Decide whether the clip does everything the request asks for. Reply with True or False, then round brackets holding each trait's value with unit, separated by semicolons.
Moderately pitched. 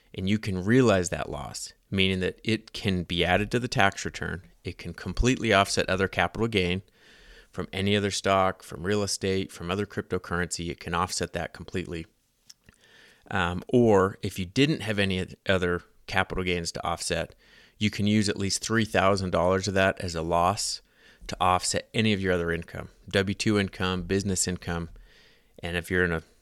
False (95 Hz)